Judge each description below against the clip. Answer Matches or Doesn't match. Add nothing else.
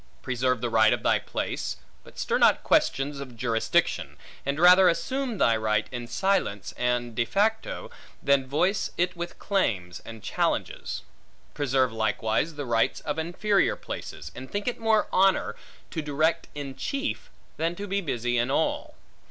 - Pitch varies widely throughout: Matches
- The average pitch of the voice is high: Doesn't match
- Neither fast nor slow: Matches